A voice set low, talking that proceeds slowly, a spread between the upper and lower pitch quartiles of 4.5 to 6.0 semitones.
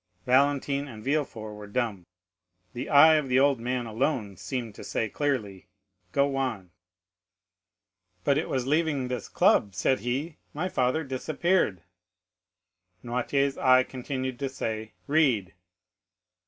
No: low, 130 Hz; slow, 130 wpm; average, 4.0 semitones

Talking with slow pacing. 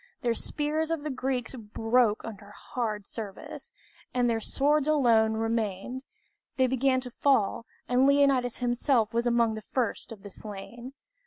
No: average, 150 wpm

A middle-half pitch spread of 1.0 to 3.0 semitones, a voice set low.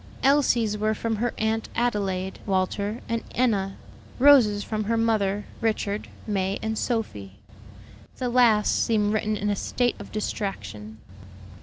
No: narrow, 2.4 semitones; high, 215 Hz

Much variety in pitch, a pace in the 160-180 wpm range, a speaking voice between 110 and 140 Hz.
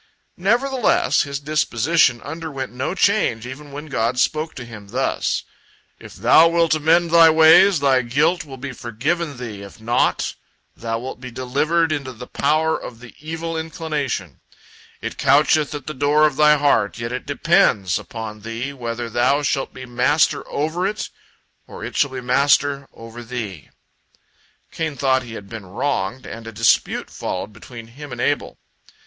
No: average, 4.6 semitones; average, 165 wpm; low, 135 Hz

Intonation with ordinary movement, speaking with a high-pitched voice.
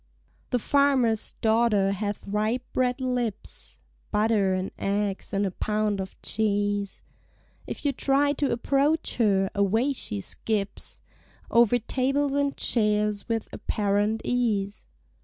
Yes: average, 3.6 semitones; high, 220 Hz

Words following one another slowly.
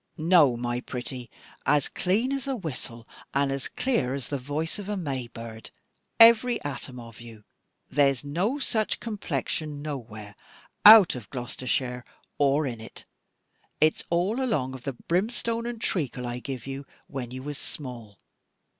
No: average, 155 wpm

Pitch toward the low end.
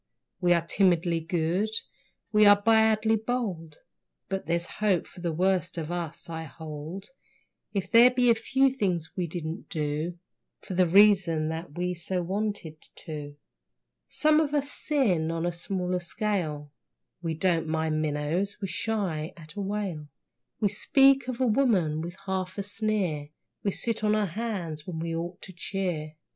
No: medium, 180 Hz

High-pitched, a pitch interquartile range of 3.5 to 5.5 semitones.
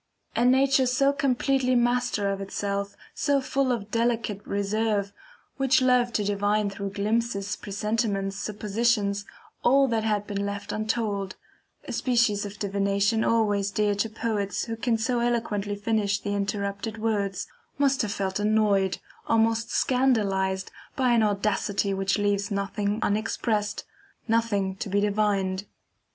No: high, 210 Hz; narrow, 2.6 semitones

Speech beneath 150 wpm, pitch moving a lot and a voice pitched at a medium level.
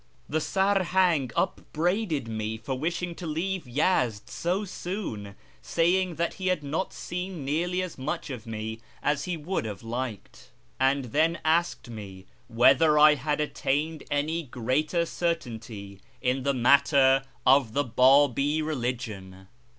Yes: slow, 135 wpm; wide, 5.8 semitones; medium, 145 Hz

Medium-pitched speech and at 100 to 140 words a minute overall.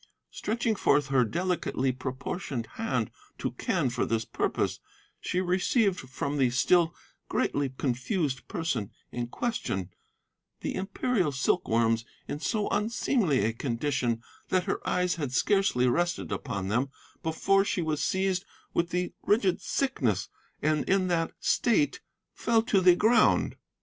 Yes: medium, 160 Hz; slow, 135 wpm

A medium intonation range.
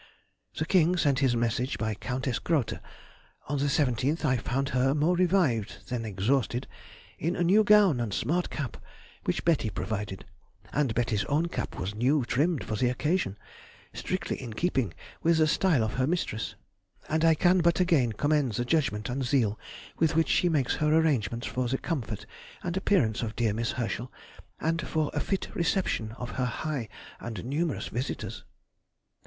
No: wide, 5.7 semitones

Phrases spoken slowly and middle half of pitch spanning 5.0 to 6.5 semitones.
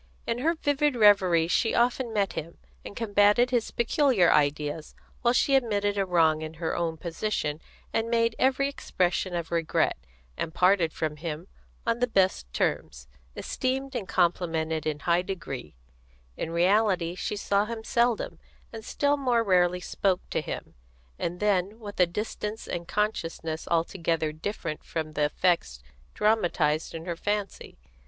No: average, 150 wpm; wide, 5.4 semitones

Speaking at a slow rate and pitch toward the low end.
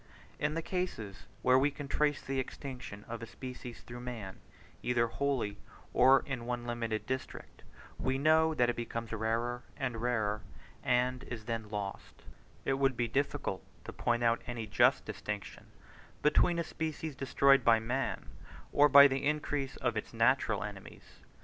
No: average, 160 wpm; low, 125 Hz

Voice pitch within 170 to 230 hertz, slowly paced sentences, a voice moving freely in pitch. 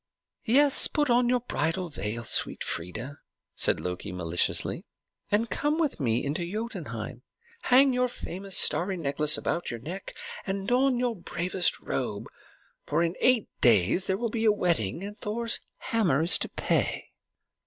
No: high, 190 Hz; average, 155 wpm; wide, 8.6 semitones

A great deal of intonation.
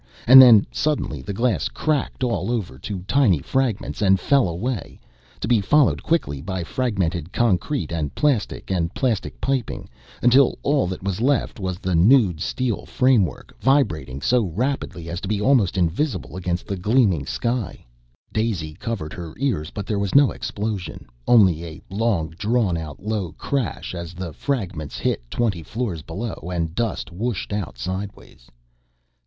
Yes: wide, 6.1 semitones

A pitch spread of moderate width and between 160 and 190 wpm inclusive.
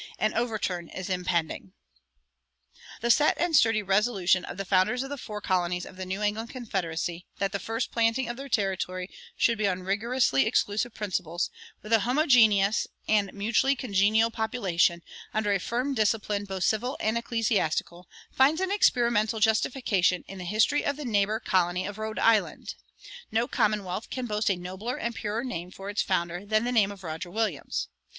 Yes: average, 3.8 semitones; average, 170 wpm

